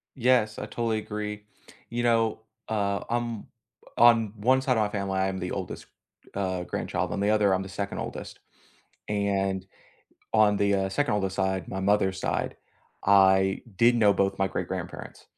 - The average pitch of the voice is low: Yes, low, 100 Hz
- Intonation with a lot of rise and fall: No, narrow, 2.5 semitones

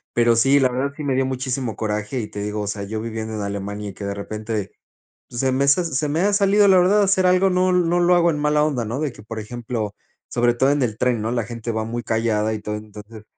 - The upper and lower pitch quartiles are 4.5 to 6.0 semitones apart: Yes, wide, 5.5 semitones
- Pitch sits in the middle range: No, low, 120 Hz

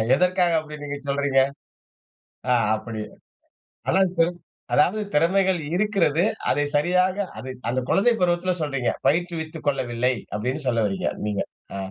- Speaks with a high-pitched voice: No, medium, 155 Hz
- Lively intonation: Yes, wide, 5.8 semitones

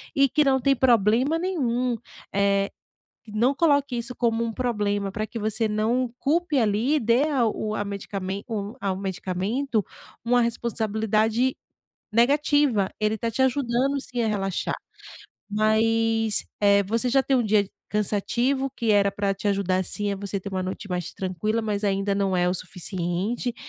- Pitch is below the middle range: No, high, 220 Hz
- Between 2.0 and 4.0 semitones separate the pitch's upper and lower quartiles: Yes, average, 3.7 semitones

